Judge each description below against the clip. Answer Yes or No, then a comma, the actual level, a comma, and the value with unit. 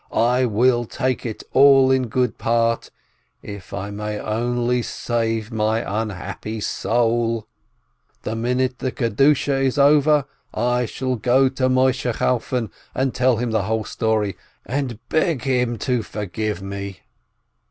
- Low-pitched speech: Yes, low, 120 Hz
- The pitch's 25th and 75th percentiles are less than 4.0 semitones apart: Yes, average, 2.9 semitones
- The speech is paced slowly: Yes, slow, 130 wpm